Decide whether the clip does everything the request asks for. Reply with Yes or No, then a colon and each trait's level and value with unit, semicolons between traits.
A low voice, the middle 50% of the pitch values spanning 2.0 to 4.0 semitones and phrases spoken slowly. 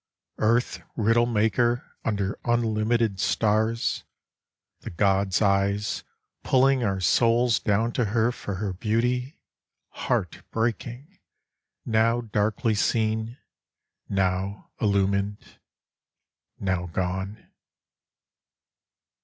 Yes: low, 110 Hz; average, 3.0 semitones; slow, 85 wpm